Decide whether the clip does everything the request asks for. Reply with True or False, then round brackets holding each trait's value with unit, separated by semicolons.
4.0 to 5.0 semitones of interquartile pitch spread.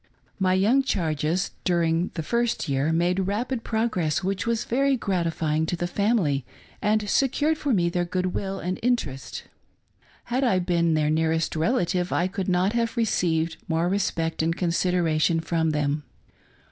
True (4.6 semitones)